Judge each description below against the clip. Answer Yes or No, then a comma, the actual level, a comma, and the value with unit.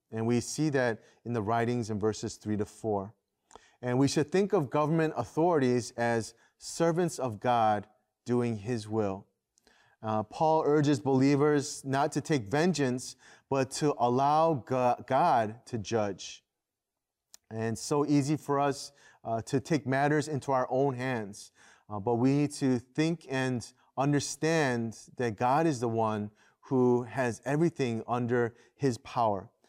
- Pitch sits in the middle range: No, low, 125 Hz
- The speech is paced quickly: No, average, 150 wpm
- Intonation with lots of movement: No, average, 4.2 semitones